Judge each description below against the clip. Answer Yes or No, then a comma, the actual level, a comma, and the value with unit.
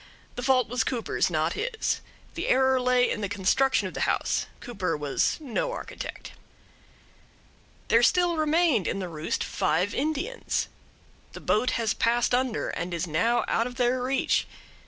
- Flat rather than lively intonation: No, average, 4.7 semitones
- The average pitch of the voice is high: Yes, high, 245 Hz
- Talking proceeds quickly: No, average, 155 wpm